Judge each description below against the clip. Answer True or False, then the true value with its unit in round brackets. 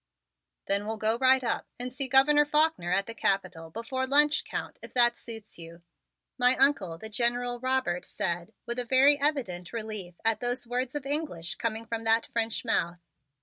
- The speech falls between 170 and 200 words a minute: True (180 wpm)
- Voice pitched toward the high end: True (235 Hz)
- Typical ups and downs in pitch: True (4.6 semitones)